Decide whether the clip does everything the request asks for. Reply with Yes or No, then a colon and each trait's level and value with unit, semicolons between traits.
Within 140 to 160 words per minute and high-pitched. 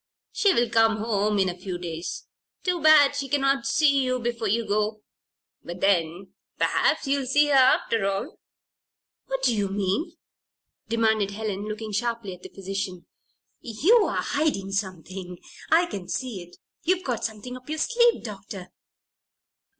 Yes: average, 150 wpm; high, 220 Hz